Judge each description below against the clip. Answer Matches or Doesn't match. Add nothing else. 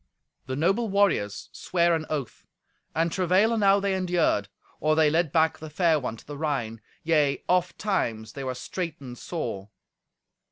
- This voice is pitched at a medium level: Matches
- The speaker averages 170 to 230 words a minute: Doesn't match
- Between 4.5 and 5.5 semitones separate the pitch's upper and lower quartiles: Matches